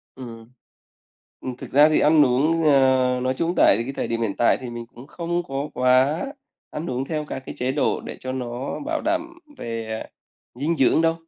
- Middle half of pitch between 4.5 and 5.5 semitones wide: No, average, 4.0 semitones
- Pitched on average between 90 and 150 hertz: Yes, low, 135 Hz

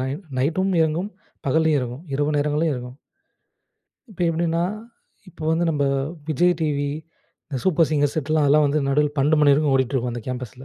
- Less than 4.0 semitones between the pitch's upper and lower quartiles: Yes, average, 2.9 semitones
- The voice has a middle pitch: Yes, medium, 150 Hz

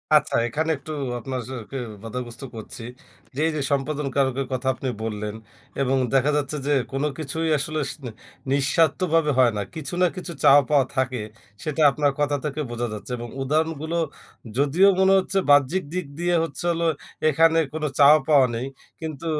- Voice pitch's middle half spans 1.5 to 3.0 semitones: No, average, 3.4 semitones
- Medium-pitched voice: Yes, medium, 145 Hz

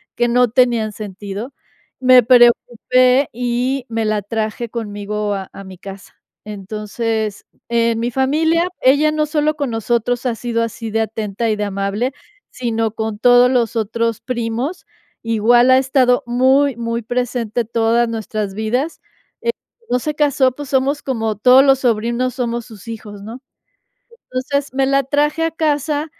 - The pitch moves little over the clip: No, average, 3.0 semitones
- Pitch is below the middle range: No, high, 240 Hz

